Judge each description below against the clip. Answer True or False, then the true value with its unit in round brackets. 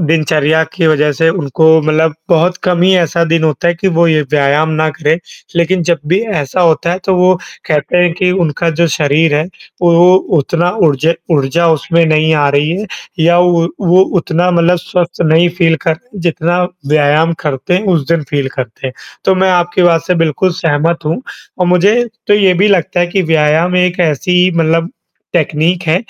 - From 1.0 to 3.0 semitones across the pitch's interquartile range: True (2.4 semitones)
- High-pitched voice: False (165 Hz)